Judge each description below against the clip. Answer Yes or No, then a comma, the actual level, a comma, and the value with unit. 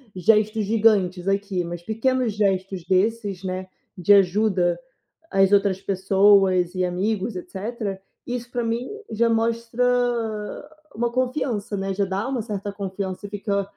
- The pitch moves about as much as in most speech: Yes, average, 3.0 semitones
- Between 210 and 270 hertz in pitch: No, high, 200 Hz